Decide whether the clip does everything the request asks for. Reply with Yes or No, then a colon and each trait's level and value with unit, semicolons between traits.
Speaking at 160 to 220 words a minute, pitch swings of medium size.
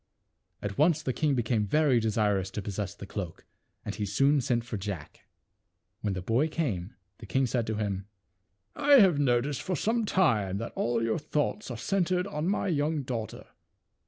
No: average, 185 wpm; wide, 6.7 semitones